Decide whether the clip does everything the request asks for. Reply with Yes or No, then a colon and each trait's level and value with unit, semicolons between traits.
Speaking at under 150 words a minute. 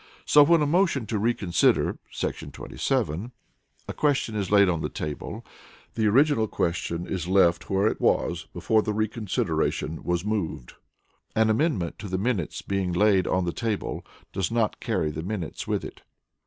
No: average, 170 wpm